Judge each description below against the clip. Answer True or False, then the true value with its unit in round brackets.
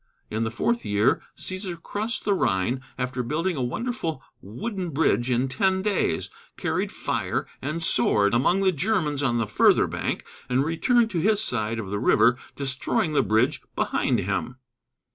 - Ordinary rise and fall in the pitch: False (8.0 semitones)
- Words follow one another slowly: False (160 wpm)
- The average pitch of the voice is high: False (140 Hz)